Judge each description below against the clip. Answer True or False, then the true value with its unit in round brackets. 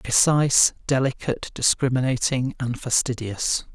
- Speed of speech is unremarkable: False (80 wpm)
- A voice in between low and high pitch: False (130 Hz)